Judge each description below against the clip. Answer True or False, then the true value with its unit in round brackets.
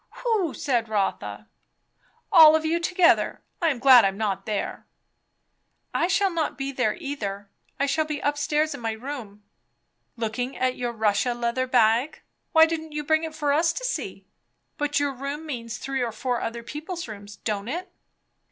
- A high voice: True (275 Hz)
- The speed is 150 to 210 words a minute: True (175 wpm)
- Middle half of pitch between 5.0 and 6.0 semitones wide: True (5.4 semitones)